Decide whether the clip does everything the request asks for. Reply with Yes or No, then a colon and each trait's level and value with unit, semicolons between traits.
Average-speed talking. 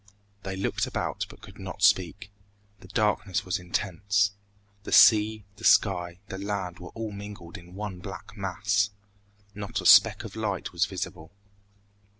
Yes: average, 150 wpm